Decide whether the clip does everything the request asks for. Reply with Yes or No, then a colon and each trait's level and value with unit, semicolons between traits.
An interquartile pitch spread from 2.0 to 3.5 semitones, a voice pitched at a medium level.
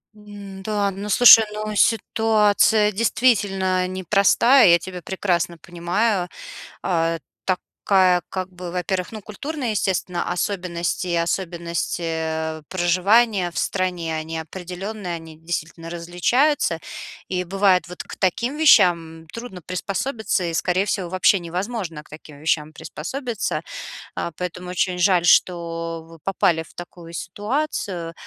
Yes: average, 3.2 semitones; medium, 180 Hz